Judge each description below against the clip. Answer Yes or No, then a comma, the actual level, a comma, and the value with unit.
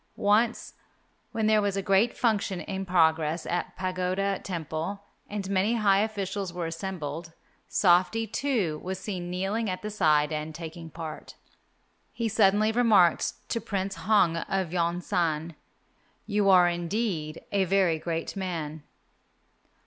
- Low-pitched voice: No, medium, 185 Hz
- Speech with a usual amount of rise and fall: Yes, average, 3.5 semitones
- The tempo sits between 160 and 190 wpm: No, slow, 135 wpm